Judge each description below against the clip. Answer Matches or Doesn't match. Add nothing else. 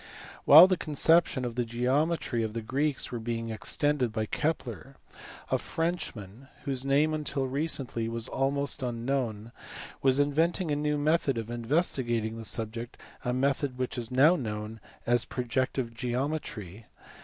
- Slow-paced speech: Doesn't match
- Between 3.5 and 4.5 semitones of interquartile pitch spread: Matches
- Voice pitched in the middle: Doesn't match